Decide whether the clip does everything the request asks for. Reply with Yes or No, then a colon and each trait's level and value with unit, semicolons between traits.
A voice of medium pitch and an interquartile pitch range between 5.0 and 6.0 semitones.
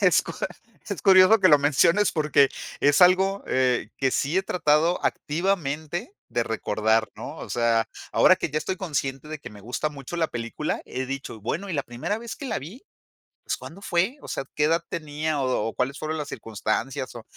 Yes: medium, 150 Hz; wide, 5.4 semitones